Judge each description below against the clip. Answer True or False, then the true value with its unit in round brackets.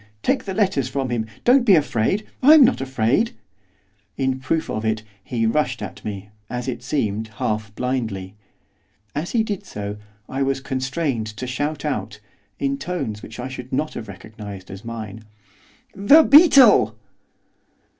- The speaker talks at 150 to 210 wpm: True (155 wpm)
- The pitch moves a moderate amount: False (6.2 semitones)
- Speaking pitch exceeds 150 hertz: False (130 Hz)